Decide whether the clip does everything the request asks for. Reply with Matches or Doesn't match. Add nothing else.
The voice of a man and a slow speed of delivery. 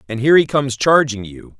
Doesn't match